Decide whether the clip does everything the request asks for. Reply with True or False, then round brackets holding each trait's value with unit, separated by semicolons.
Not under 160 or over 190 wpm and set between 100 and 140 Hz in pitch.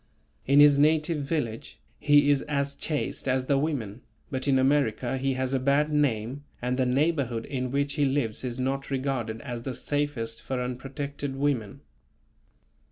True (165 wpm; 135 Hz)